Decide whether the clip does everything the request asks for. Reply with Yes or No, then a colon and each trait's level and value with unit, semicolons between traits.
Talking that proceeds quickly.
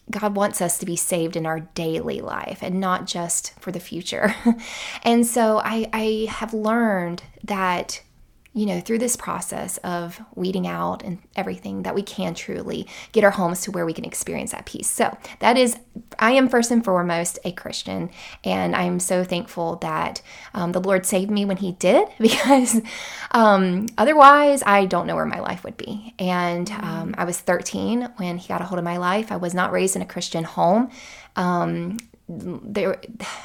No: average, 185 wpm